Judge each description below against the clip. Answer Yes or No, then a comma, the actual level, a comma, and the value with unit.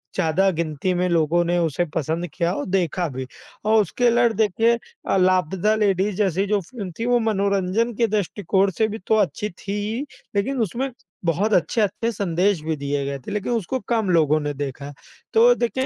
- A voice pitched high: Yes, high, 195 Hz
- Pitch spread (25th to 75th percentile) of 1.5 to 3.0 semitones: No, average, 4.6 semitones